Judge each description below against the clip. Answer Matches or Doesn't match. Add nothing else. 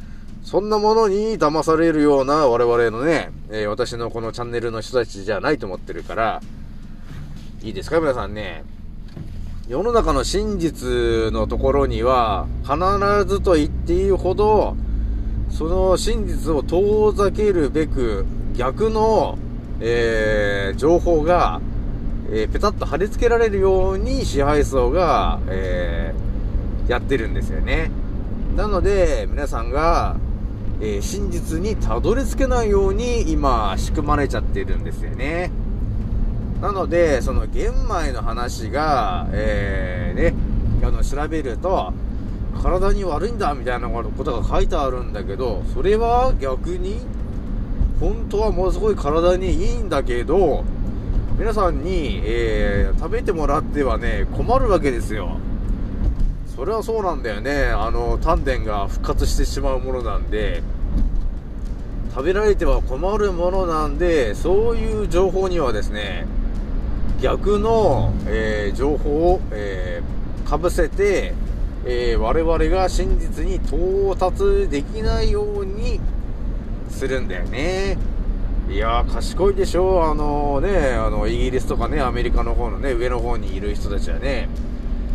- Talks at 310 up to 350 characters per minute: Doesn't match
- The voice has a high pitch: Doesn't match